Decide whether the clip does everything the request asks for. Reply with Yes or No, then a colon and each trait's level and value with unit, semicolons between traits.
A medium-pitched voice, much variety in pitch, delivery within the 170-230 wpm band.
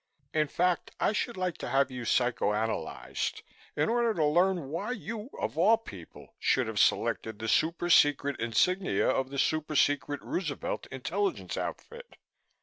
No: medium, 155 Hz; wide, 6.0 semitones; average, 155 wpm